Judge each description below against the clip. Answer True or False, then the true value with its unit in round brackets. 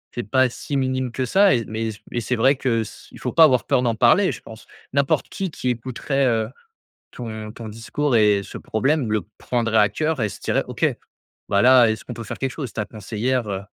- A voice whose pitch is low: True (120 Hz)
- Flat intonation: False (3.1 semitones)